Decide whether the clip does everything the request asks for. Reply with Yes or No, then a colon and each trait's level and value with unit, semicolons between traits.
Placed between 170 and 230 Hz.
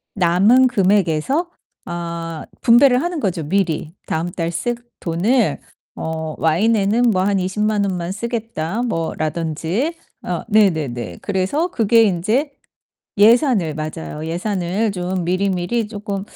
Yes: high, 190 Hz